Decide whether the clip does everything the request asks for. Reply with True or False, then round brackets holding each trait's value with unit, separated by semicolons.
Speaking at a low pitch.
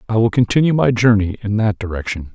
True (105 Hz)